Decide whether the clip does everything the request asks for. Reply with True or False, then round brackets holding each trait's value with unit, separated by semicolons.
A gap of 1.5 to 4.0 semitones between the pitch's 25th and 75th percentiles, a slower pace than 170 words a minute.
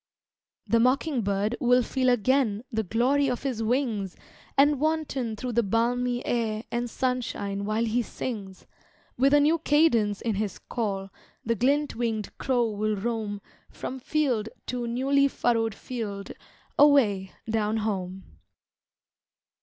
True (3.4 semitones; 135 wpm)